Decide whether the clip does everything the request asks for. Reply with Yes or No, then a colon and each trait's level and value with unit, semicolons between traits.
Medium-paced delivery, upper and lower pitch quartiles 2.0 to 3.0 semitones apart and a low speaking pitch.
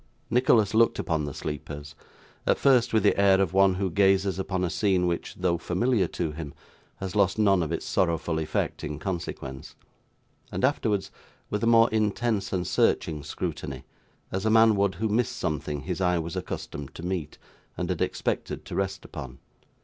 No: average, 180 wpm; average, 4.1 semitones; very low, 95 Hz